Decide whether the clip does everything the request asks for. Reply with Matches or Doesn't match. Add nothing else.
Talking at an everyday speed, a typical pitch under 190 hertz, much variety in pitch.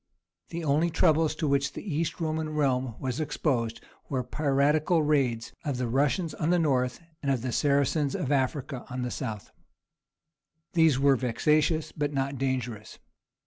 Doesn't match